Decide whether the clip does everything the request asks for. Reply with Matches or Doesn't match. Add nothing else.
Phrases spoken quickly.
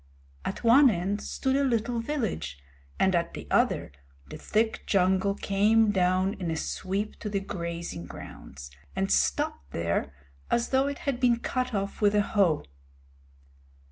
Doesn't match